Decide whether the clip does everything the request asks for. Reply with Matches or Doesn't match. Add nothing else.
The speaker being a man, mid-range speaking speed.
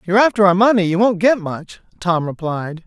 Doesn't match